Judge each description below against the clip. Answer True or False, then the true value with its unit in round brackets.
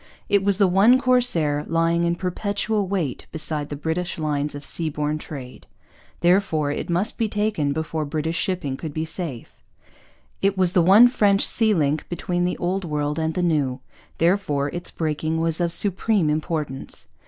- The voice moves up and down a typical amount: True (4.2 semitones)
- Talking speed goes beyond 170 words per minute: False (165 wpm)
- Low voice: False (165 Hz)